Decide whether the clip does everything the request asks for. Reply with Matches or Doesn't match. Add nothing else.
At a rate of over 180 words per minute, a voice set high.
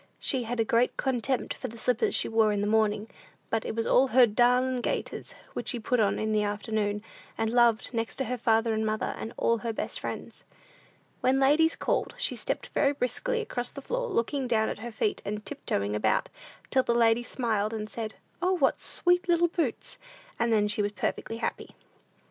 Matches